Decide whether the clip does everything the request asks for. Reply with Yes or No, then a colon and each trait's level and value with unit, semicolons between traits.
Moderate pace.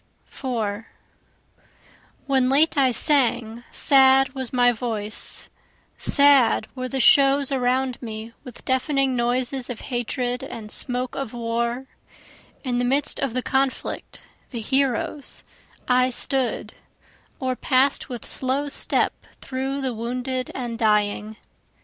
No: slow, 120 wpm